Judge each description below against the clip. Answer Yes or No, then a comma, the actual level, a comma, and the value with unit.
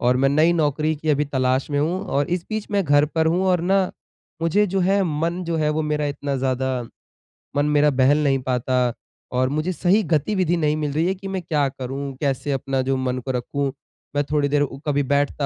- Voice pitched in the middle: Yes, medium, 145 Hz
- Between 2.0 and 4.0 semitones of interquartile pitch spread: Yes, average, 3.6 semitones